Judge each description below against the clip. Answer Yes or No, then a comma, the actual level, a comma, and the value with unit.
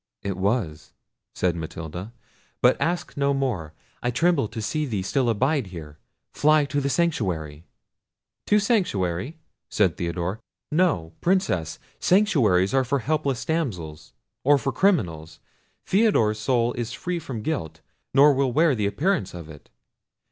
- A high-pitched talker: No, low, 120 Hz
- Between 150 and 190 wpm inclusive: No, average, 140 wpm